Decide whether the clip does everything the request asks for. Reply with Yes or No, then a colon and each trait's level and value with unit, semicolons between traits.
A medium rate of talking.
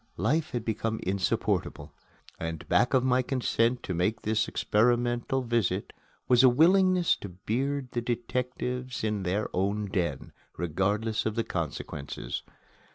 No: slow, 130 wpm